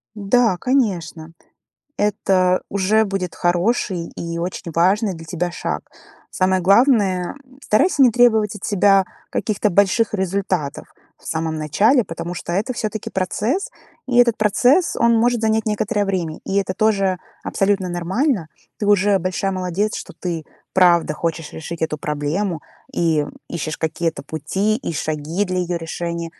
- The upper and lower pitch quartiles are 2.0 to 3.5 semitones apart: No, average, 3.9 semitones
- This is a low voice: No, high, 190 Hz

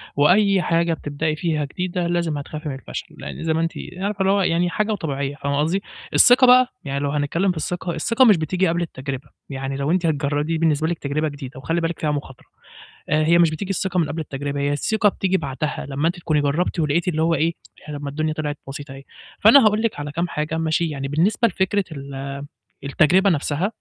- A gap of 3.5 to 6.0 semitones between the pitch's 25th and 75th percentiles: Yes, average, 3.8 semitones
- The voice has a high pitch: No, medium, 160 Hz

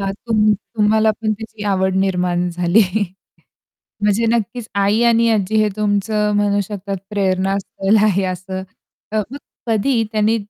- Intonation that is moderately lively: No, narrow, 2.1 semitones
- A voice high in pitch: Yes, high, 205 Hz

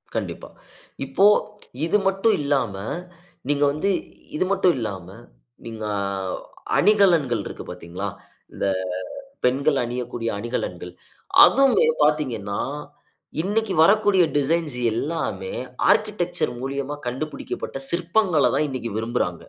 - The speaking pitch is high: No, medium, 145 Hz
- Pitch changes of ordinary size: No, wide, 7.6 semitones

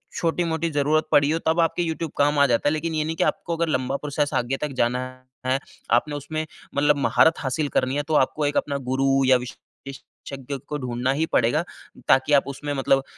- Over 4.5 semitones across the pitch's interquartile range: No, average, 2.7 semitones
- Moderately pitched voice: Yes, medium, 145 Hz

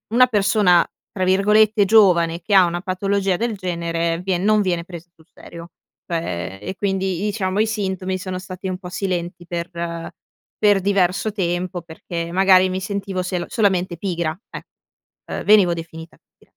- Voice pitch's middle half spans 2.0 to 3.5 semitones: Yes, narrow, 2.5 semitones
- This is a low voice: No, medium, 185 Hz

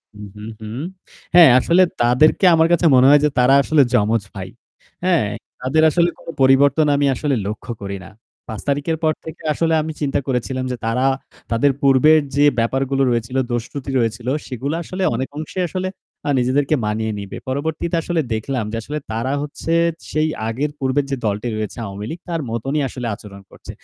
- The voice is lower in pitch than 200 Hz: Yes, low, 135 Hz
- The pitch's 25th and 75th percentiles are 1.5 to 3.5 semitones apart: No, average, 5.0 semitones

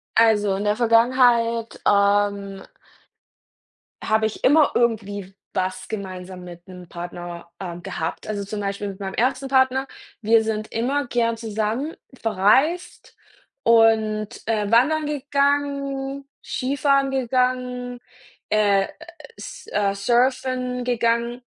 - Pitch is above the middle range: Yes, high, 225 Hz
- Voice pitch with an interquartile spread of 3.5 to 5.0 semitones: Yes, average, 4.2 semitones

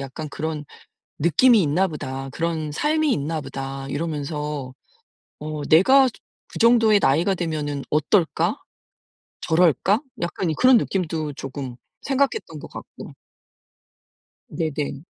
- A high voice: No, medium, 155 Hz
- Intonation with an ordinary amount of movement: Yes, average, 4.9 semitones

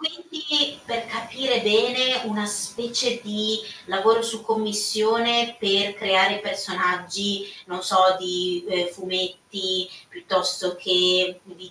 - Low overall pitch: No, high, 205 Hz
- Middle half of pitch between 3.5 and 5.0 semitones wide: Yes, average, 3.9 semitones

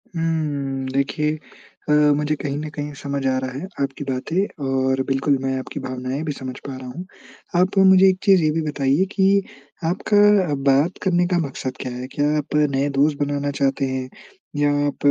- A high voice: No, medium, 145 Hz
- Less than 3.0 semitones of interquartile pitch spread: No, average, 3.5 semitones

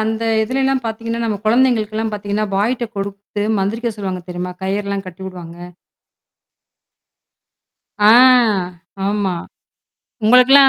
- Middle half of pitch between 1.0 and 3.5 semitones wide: Yes, average, 2.7 semitones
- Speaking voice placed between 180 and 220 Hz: Yes, high, 210 Hz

